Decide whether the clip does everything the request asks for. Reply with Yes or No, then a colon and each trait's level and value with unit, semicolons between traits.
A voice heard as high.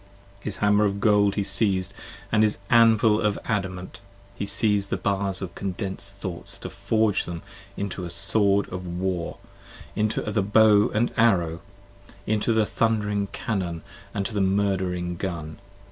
No: low, 100 Hz